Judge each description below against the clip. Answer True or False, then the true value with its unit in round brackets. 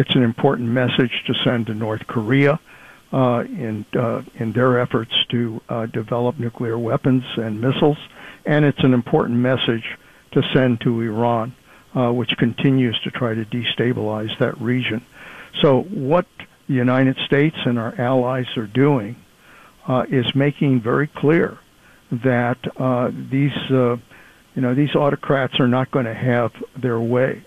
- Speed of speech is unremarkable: True (155 wpm)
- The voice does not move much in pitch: True (2.2 semitones)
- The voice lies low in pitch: True (125 Hz)